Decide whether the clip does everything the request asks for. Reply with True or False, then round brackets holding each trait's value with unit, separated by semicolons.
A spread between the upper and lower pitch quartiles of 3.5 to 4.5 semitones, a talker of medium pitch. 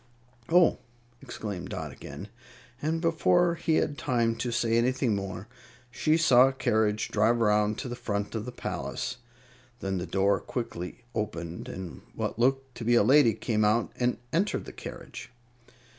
False (4.1 semitones; 115 Hz)